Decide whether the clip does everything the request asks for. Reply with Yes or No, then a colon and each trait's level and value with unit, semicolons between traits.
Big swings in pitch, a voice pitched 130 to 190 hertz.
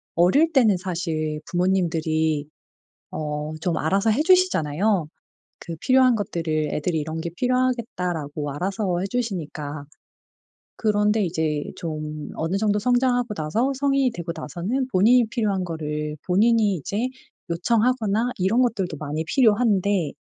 Yes: wide, 6.4 semitones; medium, 185 Hz